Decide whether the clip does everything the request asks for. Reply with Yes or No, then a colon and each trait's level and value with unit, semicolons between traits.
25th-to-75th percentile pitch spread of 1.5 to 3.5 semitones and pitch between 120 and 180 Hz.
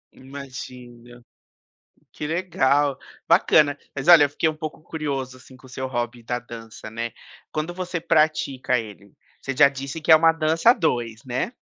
No: average, 4.2 semitones; medium, 140 Hz